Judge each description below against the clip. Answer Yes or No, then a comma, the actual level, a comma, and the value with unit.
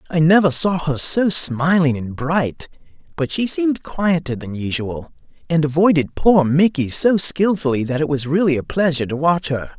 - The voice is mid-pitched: Yes, medium, 155 Hz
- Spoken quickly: No, average, 180 wpm